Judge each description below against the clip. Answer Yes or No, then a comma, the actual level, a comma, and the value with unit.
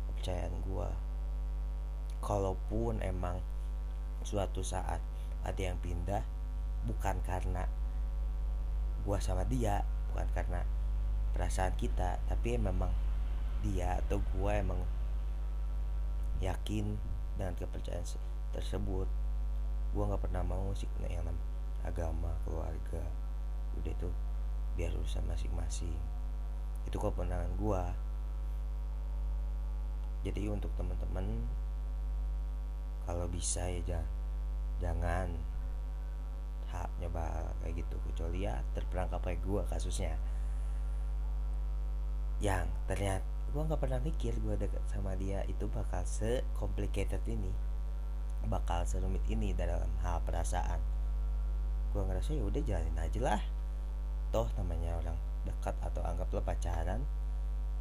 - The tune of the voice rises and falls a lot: No, average, 3.9 semitones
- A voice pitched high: No, very low, 85 Hz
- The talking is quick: No, average, 100 wpm